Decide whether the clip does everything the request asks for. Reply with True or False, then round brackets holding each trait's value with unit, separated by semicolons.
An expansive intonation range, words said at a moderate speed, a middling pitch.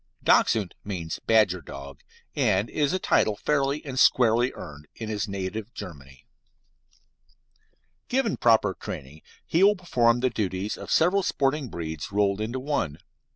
False (6.7 semitones; 145 wpm; 110 Hz)